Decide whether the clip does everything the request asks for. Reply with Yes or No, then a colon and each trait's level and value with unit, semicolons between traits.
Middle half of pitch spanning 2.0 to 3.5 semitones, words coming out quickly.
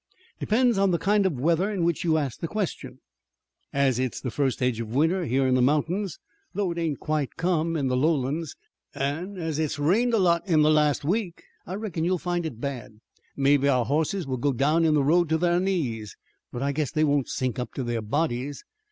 No: average, 4.3 semitones; fast, 220 wpm